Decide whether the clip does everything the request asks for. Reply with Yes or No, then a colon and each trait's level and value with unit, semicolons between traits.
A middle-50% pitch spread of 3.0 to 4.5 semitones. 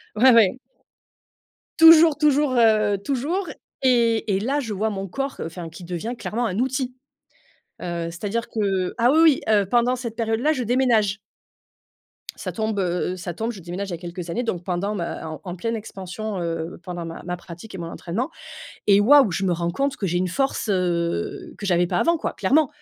No: wide, 5.6 semitones